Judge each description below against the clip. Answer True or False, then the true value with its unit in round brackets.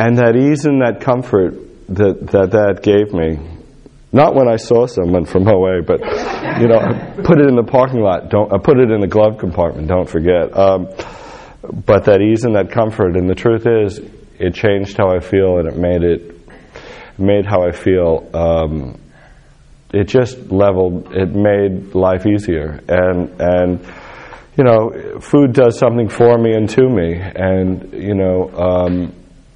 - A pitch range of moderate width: True (4.0 semitones)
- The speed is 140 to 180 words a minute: True (165 wpm)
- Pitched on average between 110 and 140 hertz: False (95 Hz)